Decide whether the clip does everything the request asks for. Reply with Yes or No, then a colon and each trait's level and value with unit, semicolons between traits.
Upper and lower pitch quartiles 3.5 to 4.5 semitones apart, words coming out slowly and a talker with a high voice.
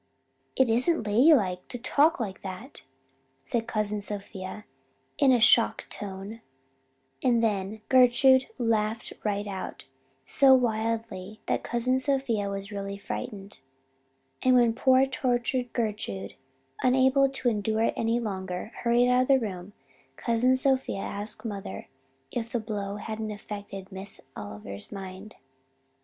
Yes: average, 3.9 semitones; slow, 130 wpm; high, 220 Hz